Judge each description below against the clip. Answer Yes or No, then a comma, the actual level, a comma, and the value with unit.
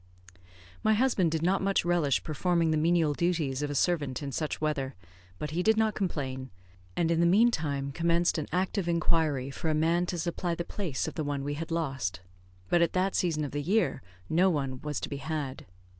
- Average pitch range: Yes, average, 3.3 semitones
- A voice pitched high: No, medium, 160 Hz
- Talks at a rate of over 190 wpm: Yes, fast, 205 wpm